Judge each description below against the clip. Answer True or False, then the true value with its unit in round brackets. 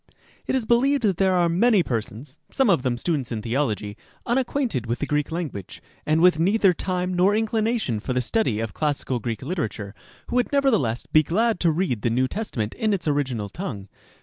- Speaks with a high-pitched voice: False (160 Hz)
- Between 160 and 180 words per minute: False (195 wpm)